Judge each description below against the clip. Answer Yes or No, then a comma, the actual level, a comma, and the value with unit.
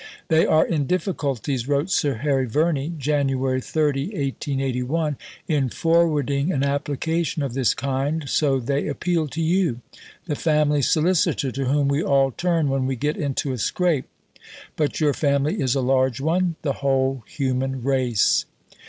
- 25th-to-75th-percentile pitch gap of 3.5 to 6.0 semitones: No, average, 2.7 semitones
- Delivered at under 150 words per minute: No, average, 155 wpm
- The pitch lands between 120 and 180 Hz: Yes, medium, 140 Hz